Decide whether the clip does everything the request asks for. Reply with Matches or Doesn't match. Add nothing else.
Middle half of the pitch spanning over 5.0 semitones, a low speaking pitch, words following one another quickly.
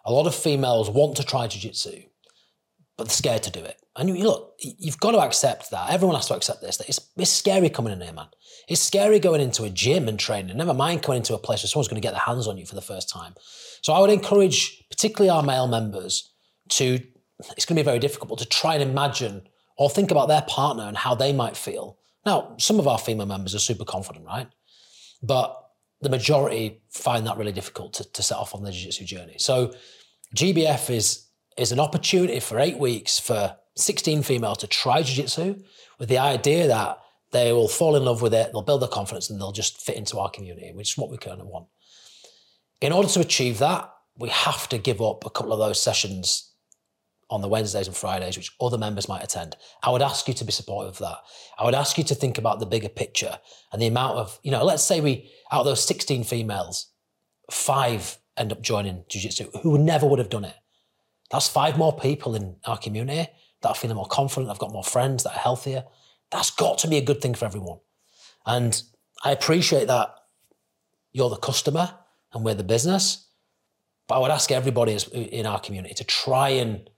Matches